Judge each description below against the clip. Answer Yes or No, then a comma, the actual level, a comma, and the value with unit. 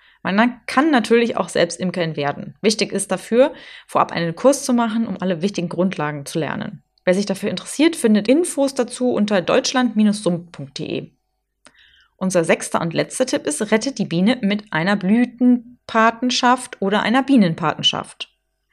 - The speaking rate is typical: Yes, average, 145 wpm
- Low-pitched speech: No, high, 215 Hz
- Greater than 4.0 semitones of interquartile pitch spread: Yes, average, 5.2 semitones